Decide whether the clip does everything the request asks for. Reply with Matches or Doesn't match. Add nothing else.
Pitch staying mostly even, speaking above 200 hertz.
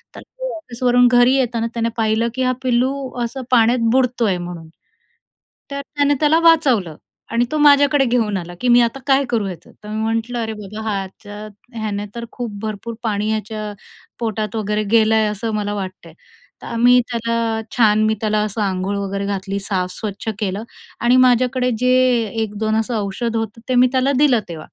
Doesn't match